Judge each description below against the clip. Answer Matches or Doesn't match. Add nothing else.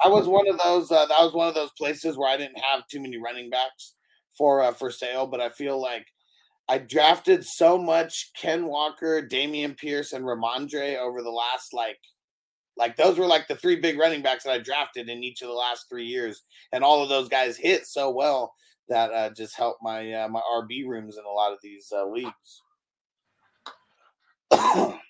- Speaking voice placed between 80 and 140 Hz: Matches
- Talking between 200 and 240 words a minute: Matches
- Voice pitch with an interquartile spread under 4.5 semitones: Doesn't match